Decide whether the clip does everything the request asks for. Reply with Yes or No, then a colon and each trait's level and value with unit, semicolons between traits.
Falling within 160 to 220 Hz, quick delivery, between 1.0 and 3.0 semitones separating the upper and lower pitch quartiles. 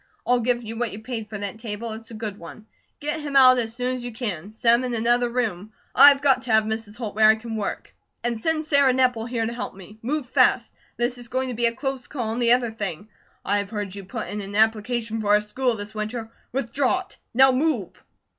No: high, 230 Hz; fast, 240 wpm; average, 2.7 semitones